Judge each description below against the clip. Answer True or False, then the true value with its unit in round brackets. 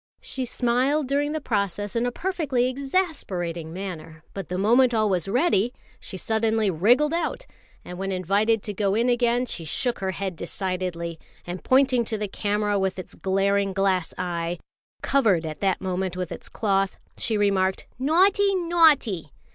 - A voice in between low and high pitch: False (205 Hz)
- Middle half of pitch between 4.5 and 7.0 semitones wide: True (5.3 semitones)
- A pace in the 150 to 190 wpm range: True (165 wpm)